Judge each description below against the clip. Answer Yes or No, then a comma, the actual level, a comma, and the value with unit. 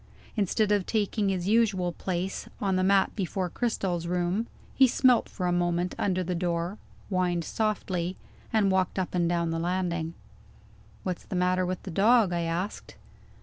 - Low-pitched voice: No, medium, 185 Hz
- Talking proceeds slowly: No, average, 165 wpm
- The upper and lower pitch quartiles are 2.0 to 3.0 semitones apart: Yes, narrow, 2.4 semitones